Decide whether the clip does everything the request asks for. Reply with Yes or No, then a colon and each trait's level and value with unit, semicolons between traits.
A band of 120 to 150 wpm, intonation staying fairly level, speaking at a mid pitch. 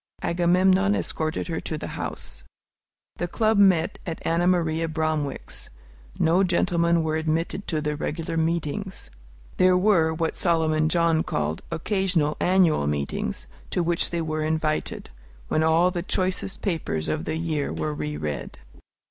Yes: average, 145 wpm; narrow, 2.3 semitones; medium, 165 Hz